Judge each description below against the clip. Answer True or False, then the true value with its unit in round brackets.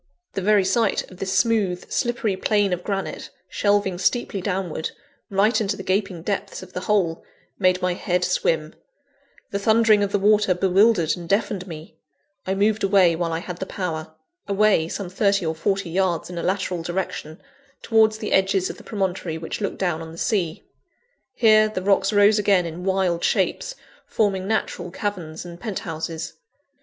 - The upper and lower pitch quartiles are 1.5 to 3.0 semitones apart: True (2.7 semitones)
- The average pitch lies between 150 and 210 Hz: True (190 Hz)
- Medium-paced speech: True (170 wpm)